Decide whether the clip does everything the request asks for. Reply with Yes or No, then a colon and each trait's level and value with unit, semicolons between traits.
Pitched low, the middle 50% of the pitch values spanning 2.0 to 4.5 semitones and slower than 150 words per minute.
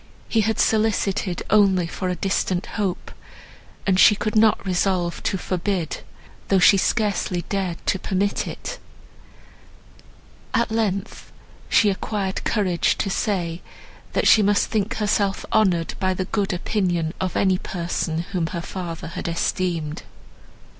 No: high, 190 Hz; narrow, 2.6 semitones; slow, 135 wpm